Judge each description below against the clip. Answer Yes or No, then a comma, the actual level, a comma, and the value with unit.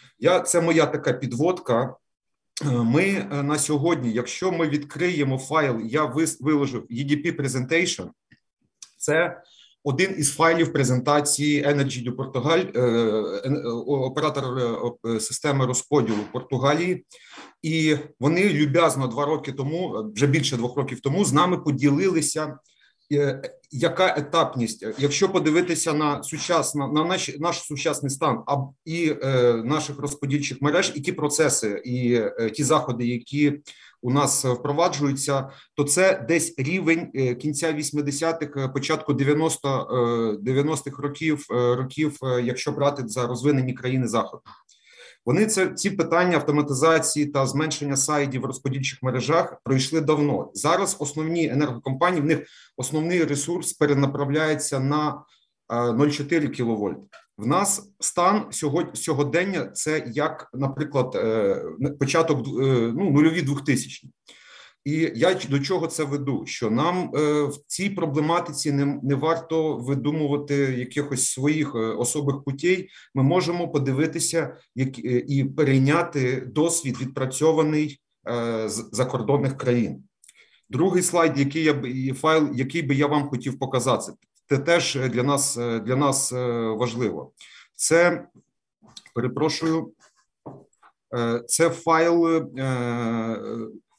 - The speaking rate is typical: Yes, average, 120 wpm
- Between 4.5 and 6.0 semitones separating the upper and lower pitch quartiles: No, average, 3.4 semitones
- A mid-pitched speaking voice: Yes, medium, 145 Hz